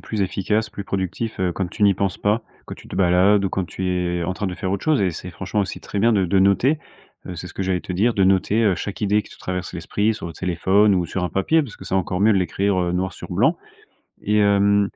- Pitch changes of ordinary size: No, narrow, 2.1 semitones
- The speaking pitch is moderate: No, very low, 95 Hz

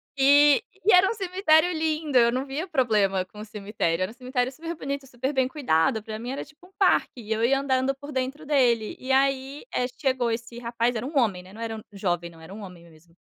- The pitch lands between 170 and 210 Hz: No, very high, 255 Hz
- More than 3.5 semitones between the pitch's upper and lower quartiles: Yes, average, 4.7 semitones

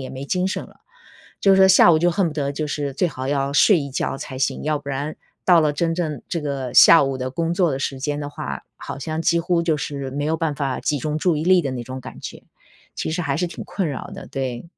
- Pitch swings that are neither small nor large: Yes, average, 3.5 semitones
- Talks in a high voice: No, medium, 150 Hz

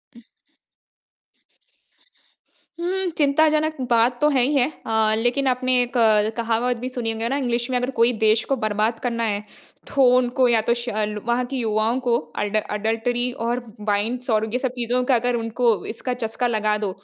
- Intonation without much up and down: Yes, narrow, 2.2 semitones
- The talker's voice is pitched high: Yes, high, 240 Hz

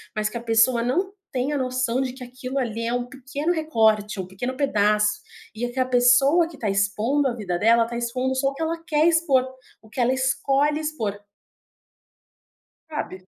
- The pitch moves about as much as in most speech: Yes, average, 3.5 semitones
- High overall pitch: Yes, very high, 255 Hz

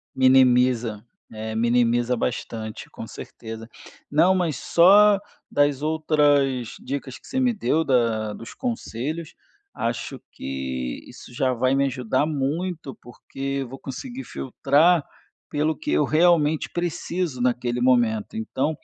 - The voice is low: Yes, low, 130 Hz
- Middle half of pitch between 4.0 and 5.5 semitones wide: Yes, average, 4.8 semitones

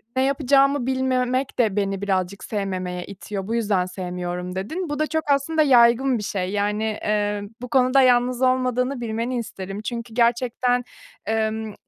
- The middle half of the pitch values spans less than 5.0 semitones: Yes, average, 4.1 semitones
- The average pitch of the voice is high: Yes, high, 235 Hz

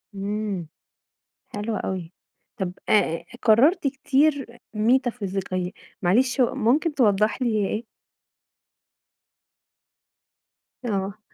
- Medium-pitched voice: No, high, 215 Hz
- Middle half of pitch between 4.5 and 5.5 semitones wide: Yes, average, 4.9 semitones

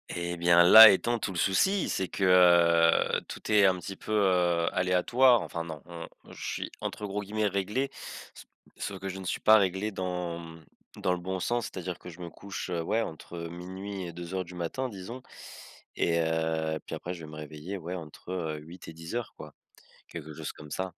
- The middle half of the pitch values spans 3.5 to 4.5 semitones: No, average, 2.8 semitones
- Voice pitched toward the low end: Yes, very low, 90 Hz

